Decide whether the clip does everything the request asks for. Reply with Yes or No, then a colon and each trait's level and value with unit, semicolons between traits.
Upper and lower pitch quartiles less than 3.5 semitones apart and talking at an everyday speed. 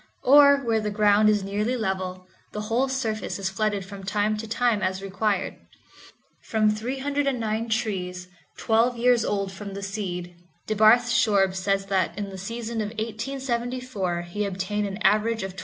Yes: average, 3.0 semitones; average, 160 wpm